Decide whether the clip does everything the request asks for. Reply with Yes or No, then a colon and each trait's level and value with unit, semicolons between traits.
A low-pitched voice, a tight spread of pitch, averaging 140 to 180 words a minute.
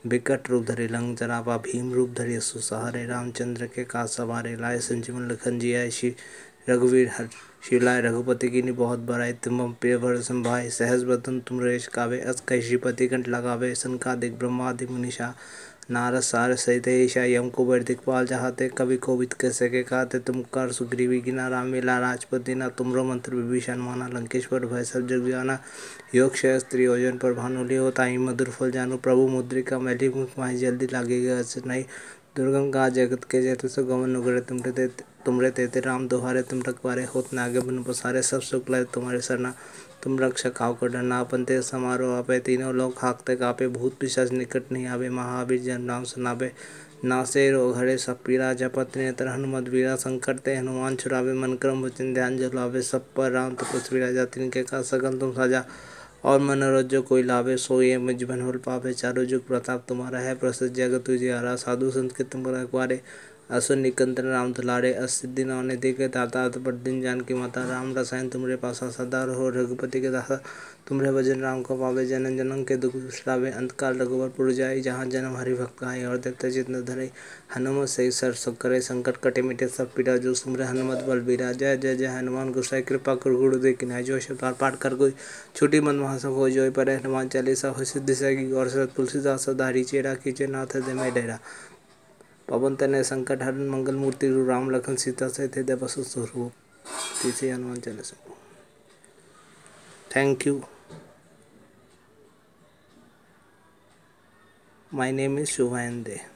Yes: low, 130 Hz; narrow, 0.8 semitones; average, 155 wpm